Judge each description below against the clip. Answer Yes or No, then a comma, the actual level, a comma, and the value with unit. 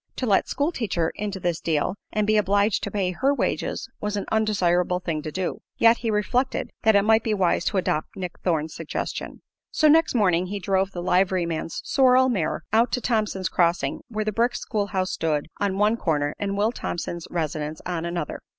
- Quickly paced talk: No, average, 195 wpm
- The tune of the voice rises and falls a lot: No, average, 4.0 semitones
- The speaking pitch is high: Yes, high, 195 Hz